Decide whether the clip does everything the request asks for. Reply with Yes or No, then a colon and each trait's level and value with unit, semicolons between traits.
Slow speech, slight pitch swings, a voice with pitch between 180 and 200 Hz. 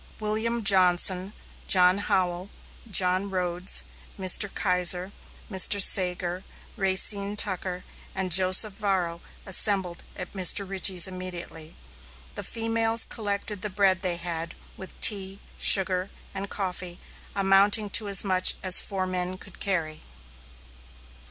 Yes: slow, 115 wpm; narrow, 1.8 semitones; high, 190 Hz